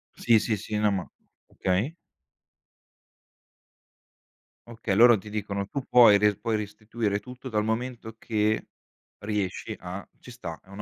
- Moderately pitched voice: No, low, 105 Hz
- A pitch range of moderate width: No, narrow, 2.3 semitones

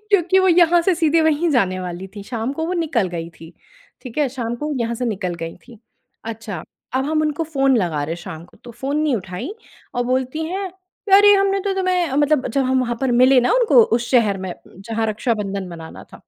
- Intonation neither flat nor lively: No, wide, 7.5 semitones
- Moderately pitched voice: No, very high, 255 Hz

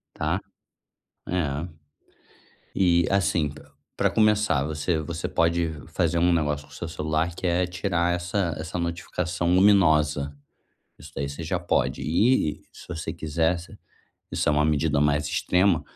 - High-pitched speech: No, very low, 85 Hz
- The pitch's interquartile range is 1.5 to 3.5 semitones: Yes, average, 2.8 semitones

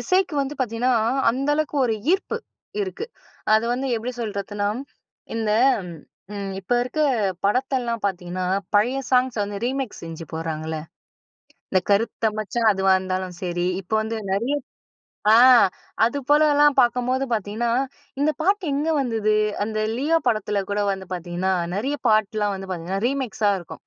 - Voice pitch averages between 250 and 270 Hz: No, high, 220 Hz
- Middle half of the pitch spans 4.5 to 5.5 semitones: Yes, average, 5.1 semitones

